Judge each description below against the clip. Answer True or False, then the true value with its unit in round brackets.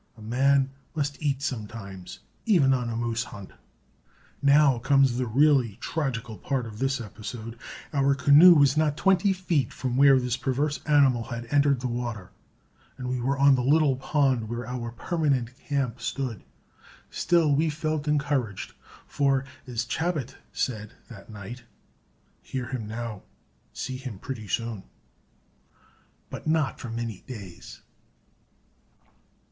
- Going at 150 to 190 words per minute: False (140 wpm)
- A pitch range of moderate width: True (3.5 semitones)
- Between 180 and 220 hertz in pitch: False (130 Hz)